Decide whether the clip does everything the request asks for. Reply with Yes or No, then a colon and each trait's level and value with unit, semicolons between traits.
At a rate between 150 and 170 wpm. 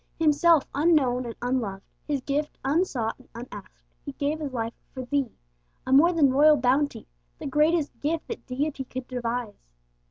Yes: average, 160 wpm